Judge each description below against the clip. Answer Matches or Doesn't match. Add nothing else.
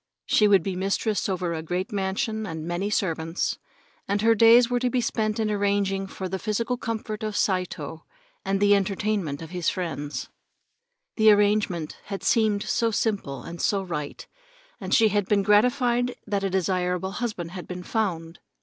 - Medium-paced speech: Matches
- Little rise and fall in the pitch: Doesn't match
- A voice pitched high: Matches